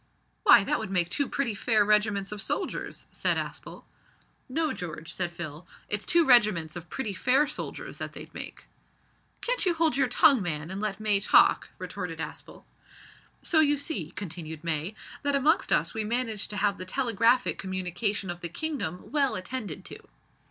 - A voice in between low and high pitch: No, high, 210 Hz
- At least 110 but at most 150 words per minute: No, average, 175 wpm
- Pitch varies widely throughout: Yes, wide, 6.8 semitones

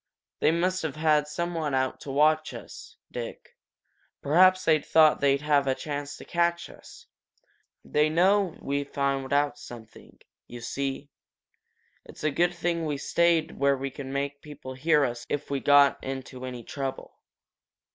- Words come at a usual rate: Yes, average, 165 wpm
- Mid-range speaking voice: Yes, medium, 145 Hz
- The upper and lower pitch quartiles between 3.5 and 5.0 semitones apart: No, average, 2.7 semitones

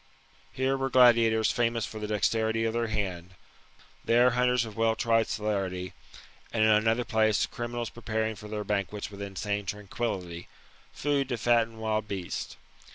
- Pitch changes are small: Yes, narrow, 2.2 semitones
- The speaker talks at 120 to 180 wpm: Yes, average, 155 wpm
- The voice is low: Yes, low, 110 Hz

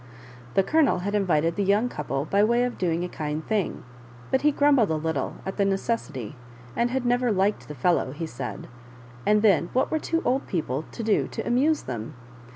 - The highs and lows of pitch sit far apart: Yes, wide, 7.3 semitones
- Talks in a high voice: Yes, high, 200 Hz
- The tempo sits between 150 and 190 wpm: No, fast, 205 wpm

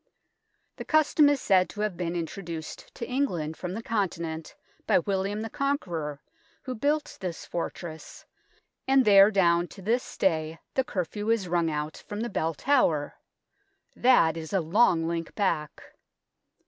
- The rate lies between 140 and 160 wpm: Yes, average, 155 wpm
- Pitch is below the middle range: No, medium, 185 Hz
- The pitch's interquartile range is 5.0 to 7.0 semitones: Yes, wide, 5.5 semitones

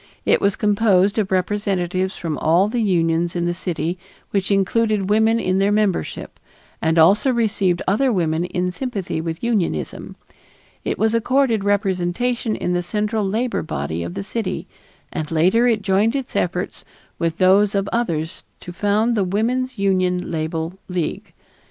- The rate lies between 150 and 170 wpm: Yes, average, 155 wpm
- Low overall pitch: No, high, 195 Hz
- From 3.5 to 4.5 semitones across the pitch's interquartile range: Yes, average, 3.8 semitones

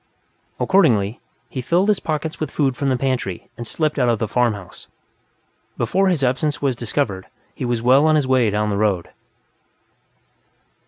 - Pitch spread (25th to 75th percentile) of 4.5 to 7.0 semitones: Yes, average, 5.2 semitones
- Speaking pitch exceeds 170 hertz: No, low, 130 Hz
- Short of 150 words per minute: No, average, 165 wpm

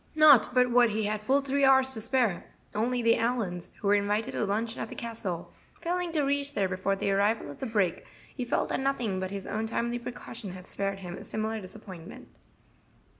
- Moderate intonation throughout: Yes, average, 4.1 semitones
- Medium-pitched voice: No, high, 225 Hz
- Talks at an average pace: No, fast, 210 wpm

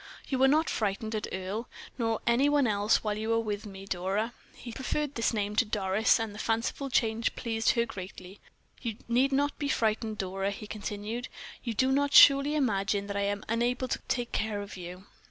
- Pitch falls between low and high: No, high, 220 Hz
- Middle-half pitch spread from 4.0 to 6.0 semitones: No, average, 3.3 semitones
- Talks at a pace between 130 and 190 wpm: No, average, 200 wpm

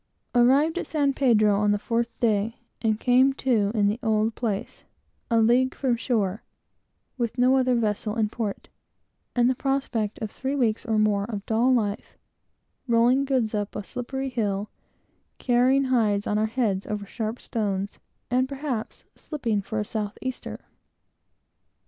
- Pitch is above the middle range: Yes, high, 230 Hz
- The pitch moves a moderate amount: Yes, average, 3.4 semitones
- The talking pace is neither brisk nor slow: Yes, average, 155 wpm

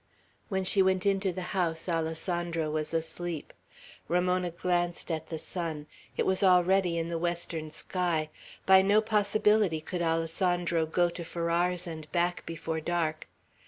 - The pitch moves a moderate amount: No, narrow, 2.0 semitones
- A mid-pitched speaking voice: Yes, medium, 175 Hz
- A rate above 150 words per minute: No, average, 145 wpm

